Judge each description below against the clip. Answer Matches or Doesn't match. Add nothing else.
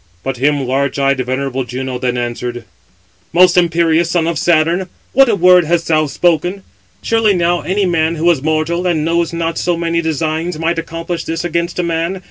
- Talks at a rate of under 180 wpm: Doesn't match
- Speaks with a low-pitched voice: Doesn't match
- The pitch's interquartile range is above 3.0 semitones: Doesn't match